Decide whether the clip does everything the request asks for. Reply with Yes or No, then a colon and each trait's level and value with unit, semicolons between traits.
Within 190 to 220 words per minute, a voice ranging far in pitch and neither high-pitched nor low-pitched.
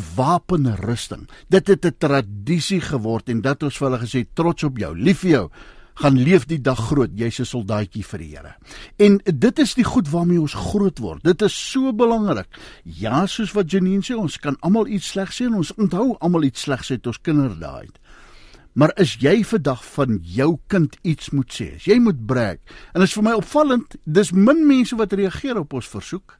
Yes: average, 200 wpm; wide, 7.9 semitones; medium, 165 Hz